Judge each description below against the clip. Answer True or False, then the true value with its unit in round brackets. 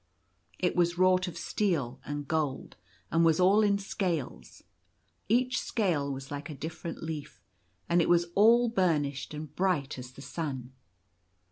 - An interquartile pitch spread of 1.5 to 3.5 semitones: False (4.5 semitones)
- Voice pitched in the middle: True (165 Hz)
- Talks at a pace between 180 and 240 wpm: False (155 wpm)